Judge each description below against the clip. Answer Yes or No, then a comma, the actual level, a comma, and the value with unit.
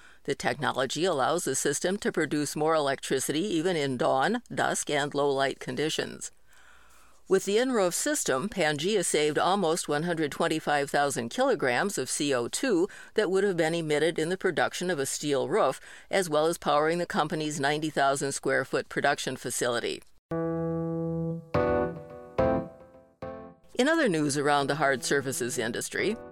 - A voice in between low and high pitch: Yes, medium, 160 Hz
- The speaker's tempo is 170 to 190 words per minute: No, slow, 135 wpm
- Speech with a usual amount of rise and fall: Yes, average, 4.3 semitones